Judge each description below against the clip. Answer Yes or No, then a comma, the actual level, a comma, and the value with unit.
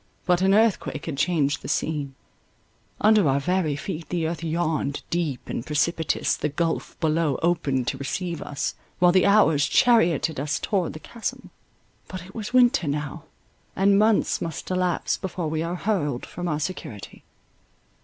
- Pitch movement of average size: Yes, average, 4.0 semitones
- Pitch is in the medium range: Yes, medium, 165 Hz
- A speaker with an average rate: Yes, average, 155 wpm